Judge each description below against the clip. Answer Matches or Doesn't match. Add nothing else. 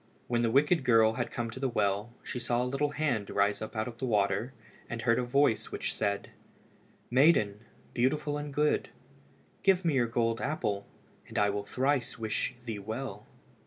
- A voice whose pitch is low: Matches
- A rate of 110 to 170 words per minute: Doesn't match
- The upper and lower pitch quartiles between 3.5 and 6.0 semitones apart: Matches